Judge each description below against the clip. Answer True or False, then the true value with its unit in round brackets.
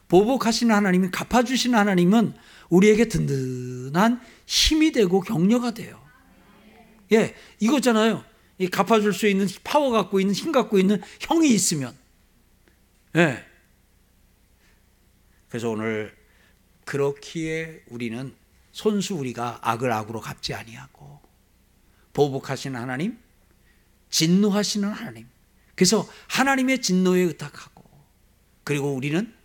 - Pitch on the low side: False (185 Hz)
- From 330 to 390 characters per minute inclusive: False (260 characters per minute)